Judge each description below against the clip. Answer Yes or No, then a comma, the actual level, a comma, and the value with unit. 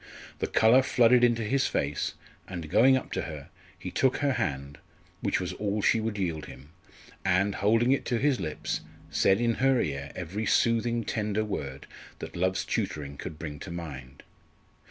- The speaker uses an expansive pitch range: Yes, wide, 7.3 semitones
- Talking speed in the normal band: Yes, average, 175 wpm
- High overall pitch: No, low, 100 Hz